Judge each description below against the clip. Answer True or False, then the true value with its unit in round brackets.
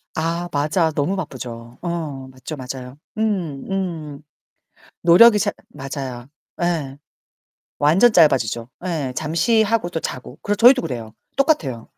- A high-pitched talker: False (155 Hz)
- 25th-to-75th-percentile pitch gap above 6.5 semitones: False (5.9 semitones)